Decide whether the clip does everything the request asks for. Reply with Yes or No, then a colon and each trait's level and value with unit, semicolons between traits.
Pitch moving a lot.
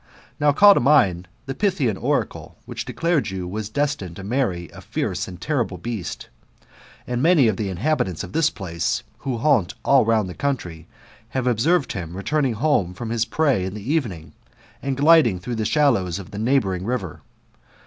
Yes: wide, 7.3 semitones